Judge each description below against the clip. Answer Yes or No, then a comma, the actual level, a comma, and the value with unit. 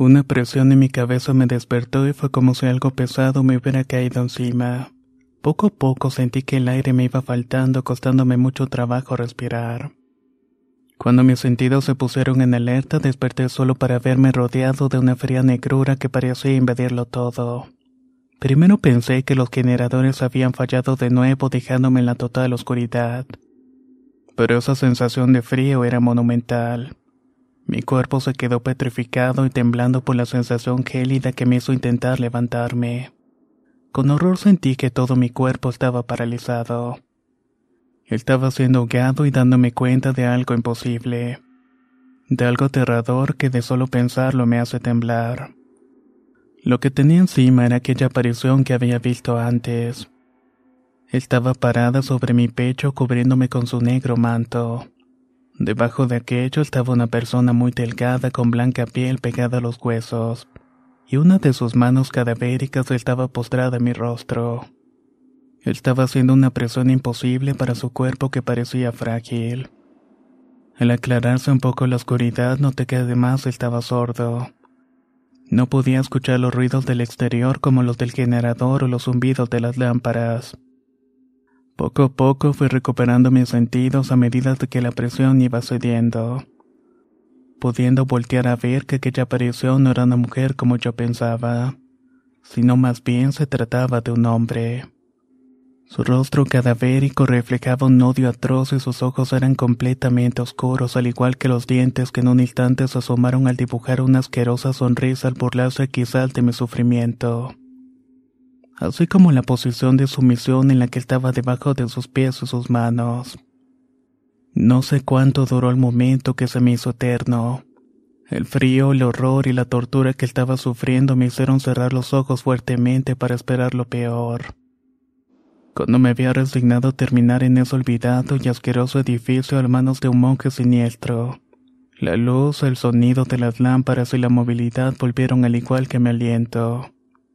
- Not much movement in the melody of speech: Yes, narrow, 1.4 semitones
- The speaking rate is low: No, average, 155 wpm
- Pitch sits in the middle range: No, low, 125 Hz